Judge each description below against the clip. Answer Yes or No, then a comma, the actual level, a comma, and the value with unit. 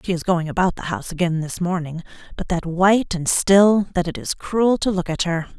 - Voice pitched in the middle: Yes, medium, 180 Hz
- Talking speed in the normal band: No, fast, 235 wpm